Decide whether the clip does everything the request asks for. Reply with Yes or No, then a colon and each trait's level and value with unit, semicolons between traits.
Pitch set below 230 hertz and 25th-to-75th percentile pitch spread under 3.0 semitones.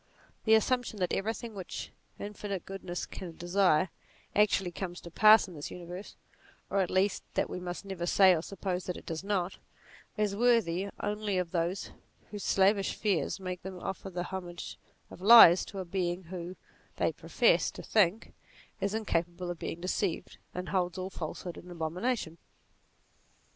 Yes: medium, 185 Hz; narrow, 2.4 semitones